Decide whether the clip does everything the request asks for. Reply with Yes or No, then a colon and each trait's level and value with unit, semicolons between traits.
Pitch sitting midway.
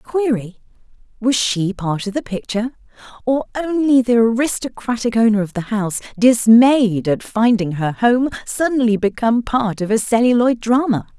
No: high, 230 Hz